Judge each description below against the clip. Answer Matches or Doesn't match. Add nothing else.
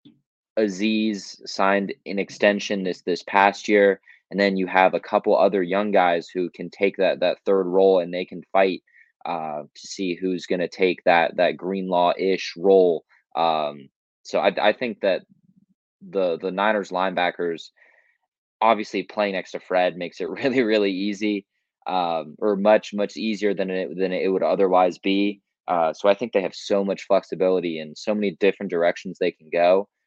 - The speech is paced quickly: Doesn't match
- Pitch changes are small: Matches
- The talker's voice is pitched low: Matches